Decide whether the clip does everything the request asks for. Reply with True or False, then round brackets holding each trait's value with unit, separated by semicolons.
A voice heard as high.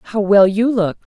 True (205 Hz)